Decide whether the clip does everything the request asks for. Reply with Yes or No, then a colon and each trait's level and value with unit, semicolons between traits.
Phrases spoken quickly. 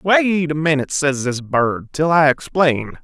No: average, 180 wpm